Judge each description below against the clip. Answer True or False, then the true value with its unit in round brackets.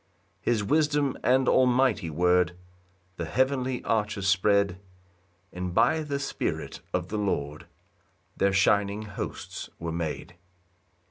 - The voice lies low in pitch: True (100 Hz)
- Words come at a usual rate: False (120 wpm)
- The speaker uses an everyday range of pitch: False (6.3 semitones)